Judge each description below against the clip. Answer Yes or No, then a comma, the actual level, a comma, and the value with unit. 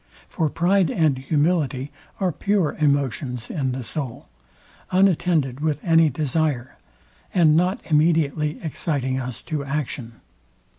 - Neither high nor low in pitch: Yes, medium, 150 Hz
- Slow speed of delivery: Yes, slow, 115 wpm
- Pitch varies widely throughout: No, average, 3.6 semitones